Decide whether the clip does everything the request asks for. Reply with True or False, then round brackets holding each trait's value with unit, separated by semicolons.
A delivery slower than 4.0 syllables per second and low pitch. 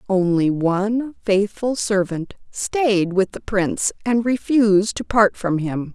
False (3.8 syllables/s; 205 Hz)